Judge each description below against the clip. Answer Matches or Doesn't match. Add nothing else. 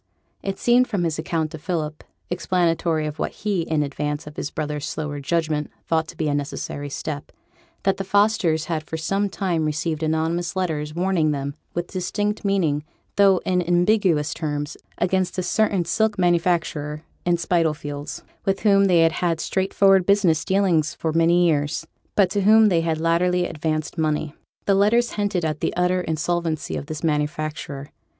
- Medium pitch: Matches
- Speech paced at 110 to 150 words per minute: Doesn't match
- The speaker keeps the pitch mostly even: Doesn't match